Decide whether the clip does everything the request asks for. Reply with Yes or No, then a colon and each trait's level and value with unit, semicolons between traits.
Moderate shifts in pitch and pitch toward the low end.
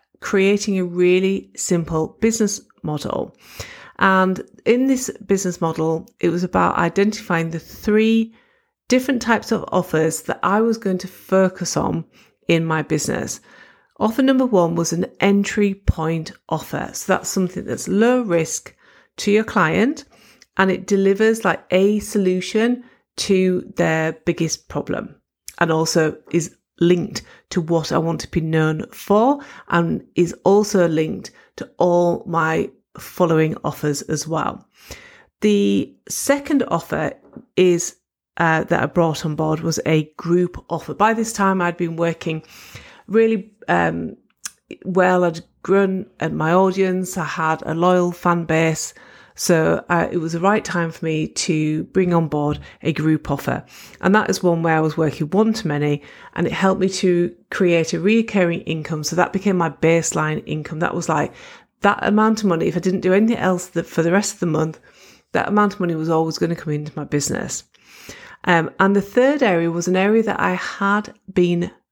No: average, 3.9 semitones; medium, 180 Hz